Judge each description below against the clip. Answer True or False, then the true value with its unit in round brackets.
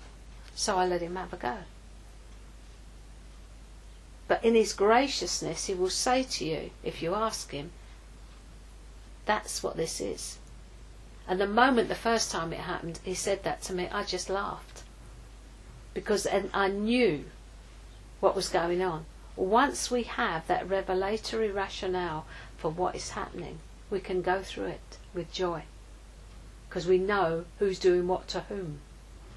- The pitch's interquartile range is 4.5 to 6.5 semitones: False (3.8 semitones)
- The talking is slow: False (145 wpm)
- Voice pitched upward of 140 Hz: True (185 Hz)